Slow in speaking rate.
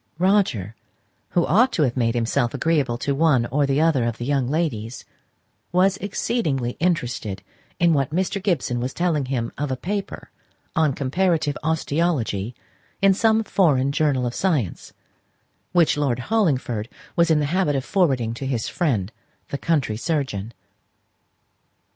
No: average, 150 wpm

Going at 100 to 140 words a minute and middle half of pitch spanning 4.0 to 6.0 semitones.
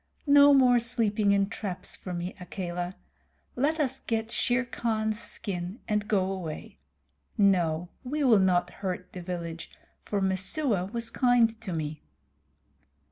Yes: slow, 135 wpm; average, 4.6 semitones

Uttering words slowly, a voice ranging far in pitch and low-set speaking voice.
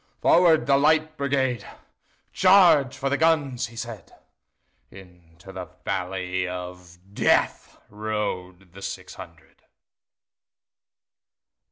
Yes: slow, 80 wpm; wide, 7.6 semitones; low, 110 Hz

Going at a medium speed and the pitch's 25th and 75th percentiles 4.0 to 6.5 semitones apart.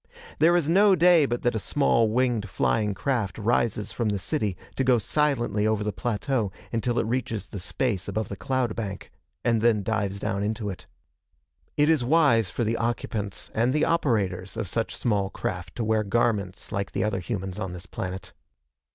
No: average, 185 wpm; average, 3.6 semitones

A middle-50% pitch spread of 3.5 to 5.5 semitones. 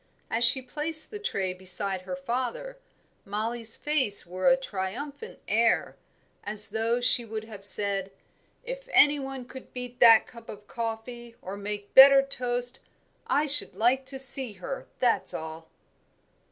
Yes: average, 4.5 semitones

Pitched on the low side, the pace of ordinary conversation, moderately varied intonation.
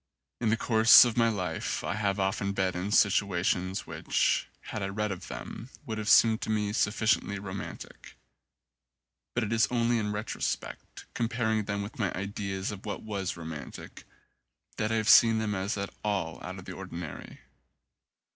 No: low, 105 Hz; average, 170 wpm; narrow, 2.3 semitones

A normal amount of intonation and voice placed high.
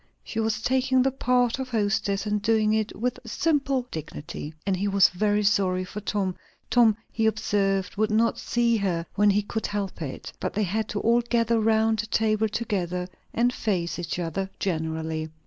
Yes: average, 3.0 semitones; high, 210 Hz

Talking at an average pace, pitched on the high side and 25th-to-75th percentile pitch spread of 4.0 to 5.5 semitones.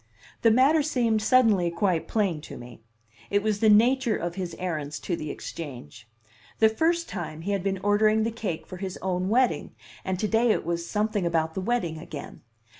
Yes: average, 190 wpm; high, 200 Hz; average, 4.6 semitones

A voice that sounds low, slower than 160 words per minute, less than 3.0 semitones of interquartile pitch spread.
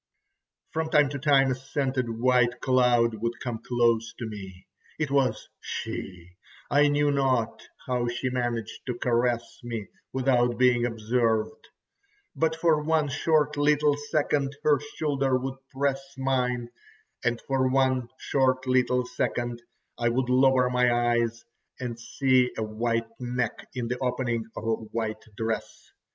Yes: low, 125 Hz; average, 145 wpm; narrow, 2.4 semitones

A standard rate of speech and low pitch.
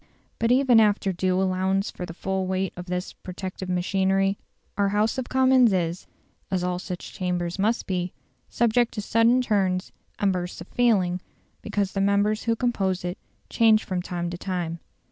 No: average, 170 wpm; high, 190 Hz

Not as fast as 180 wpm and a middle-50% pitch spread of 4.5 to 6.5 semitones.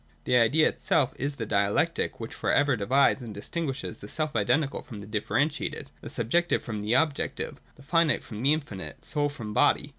No: average, 185 wpm; wide, 5.6 semitones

